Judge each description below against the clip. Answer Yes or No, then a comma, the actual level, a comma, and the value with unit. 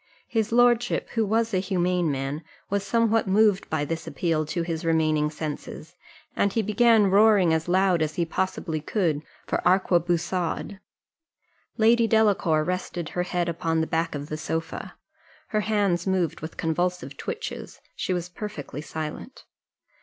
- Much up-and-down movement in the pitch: No, average, 4.3 semitones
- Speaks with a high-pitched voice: No, medium, 180 Hz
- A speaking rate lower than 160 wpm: Yes, average, 150 wpm